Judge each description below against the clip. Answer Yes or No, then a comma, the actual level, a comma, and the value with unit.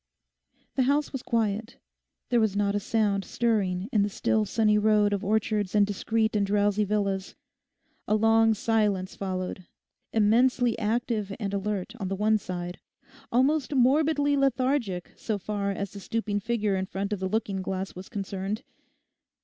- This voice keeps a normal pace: Yes, average, 155 wpm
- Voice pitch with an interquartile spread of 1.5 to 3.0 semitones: Yes, narrow, 2.4 semitones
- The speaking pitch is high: Yes, high, 210 Hz